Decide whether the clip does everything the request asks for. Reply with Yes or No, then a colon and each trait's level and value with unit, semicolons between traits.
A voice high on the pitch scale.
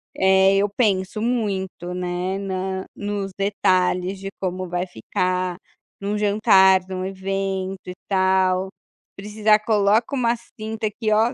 Yes: high, 195 Hz